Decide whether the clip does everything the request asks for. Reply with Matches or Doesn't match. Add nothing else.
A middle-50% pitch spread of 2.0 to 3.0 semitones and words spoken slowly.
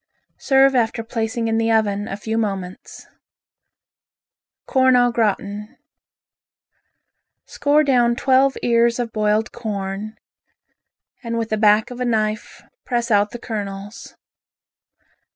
Matches